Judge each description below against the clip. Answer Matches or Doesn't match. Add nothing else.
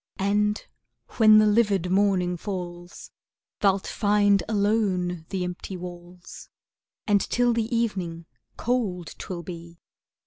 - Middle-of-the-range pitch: Doesn't match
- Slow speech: Matches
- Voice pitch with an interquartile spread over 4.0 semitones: Doesn't match